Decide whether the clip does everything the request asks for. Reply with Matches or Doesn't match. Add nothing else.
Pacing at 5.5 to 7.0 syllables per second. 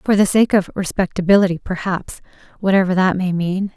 Matches